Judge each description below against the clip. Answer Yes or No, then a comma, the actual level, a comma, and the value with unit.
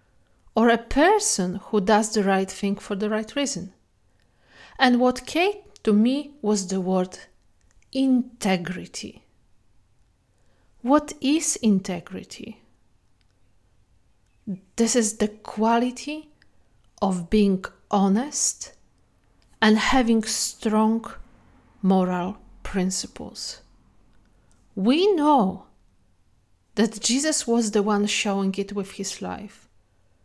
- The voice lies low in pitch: No, high, 205 Hz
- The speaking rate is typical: No, slow, 95 wpm